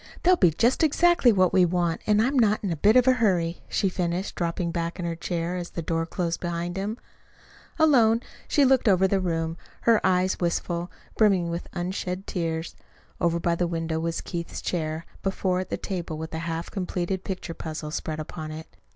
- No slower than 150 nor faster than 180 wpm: No, average, 195 wpm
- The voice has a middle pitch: Yes, medium, 175 Hz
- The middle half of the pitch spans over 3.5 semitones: No, average, 2.9 semitones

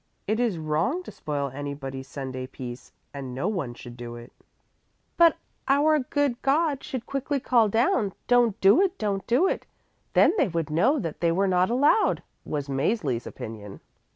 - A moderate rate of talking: Yes, average, 170 wpm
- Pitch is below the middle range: No, high, 190 Hz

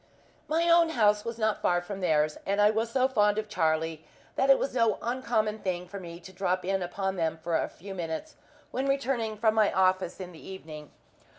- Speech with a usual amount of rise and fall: Yes, average, 4.5 semitones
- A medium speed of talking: No, fast, 210 wpm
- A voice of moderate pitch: No, high, 200 Hz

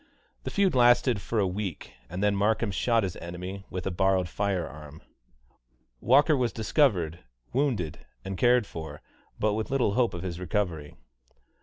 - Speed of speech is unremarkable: Yes, average, 160 wpm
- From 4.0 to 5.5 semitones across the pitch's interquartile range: Yes, average, 5.2 semitones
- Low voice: Yes, low, 100 Hz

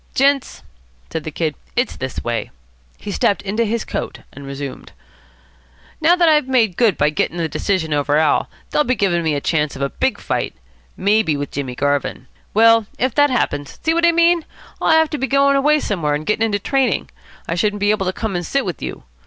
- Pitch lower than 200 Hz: No, high, 205 Hz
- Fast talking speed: Yes, fast, 210 wpm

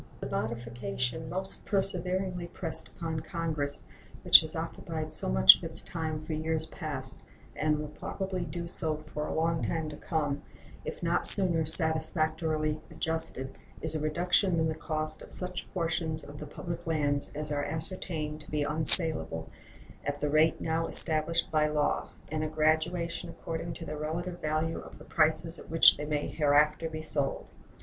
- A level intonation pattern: Yes, narrow, 1.7 semitones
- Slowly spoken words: No, average, 170 wpm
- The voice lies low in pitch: No, medium, 155 Hz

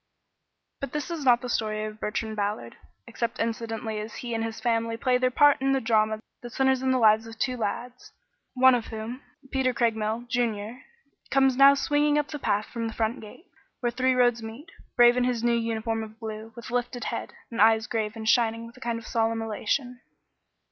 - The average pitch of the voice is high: Yes, high, 230 Hz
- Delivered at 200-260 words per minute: Yes, fast, 205 wpm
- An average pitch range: No, narrow, 2.2 semitones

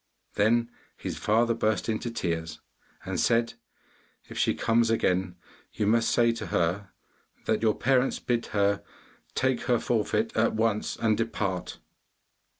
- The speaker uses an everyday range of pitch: No, narrow, 2.3 semitones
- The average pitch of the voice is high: No, low, 110 Hz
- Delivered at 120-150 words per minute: Yes, average, 140 wpm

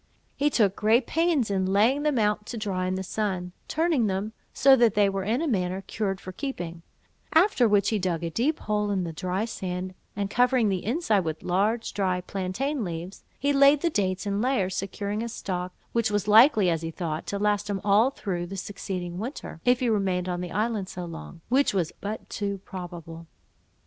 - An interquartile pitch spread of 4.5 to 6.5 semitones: No, average, 4.1 semitones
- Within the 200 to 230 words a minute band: Yes, fast, 205 wpm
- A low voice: No, high, 200 Hz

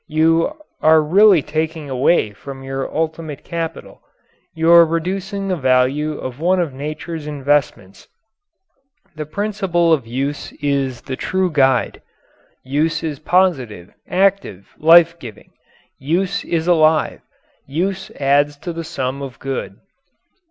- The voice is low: No, medium, 155 Hz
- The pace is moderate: No, slow, 125 wpm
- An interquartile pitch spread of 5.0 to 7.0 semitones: No, average, 3.9 semitones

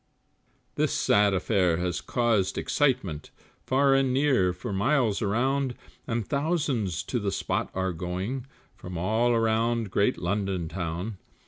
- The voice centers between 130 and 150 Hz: No, low, 105 Hz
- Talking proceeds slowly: Yes, slow, 130 wpm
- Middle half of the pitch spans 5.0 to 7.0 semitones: Yes, wide, 5.5 semitones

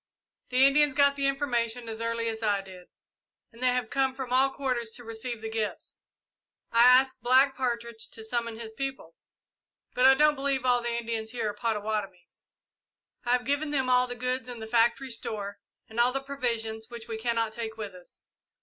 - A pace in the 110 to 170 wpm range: No, average, 195 wpm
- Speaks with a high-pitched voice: Yes, high, 240 Hz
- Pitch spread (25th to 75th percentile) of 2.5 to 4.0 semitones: Yes, average, 2.8 semitones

